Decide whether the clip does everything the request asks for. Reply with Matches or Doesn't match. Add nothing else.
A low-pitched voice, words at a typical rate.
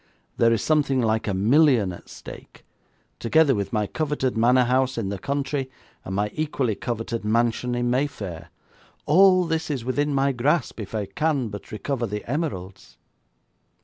Matches